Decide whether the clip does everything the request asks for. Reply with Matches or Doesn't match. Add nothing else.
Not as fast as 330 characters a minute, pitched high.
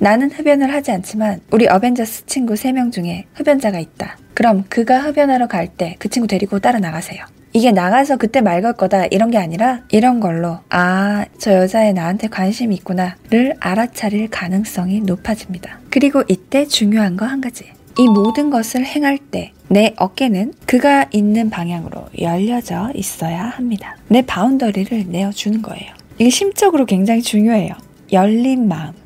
Doesn't match